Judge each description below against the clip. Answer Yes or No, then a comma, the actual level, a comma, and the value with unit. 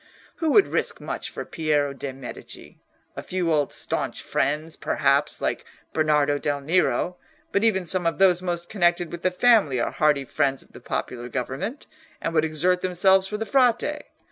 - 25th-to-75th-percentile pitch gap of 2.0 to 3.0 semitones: No, average, 4.5 semitones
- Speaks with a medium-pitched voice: Yes, medium, 170 Hz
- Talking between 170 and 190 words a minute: Yes, average, 175 wpm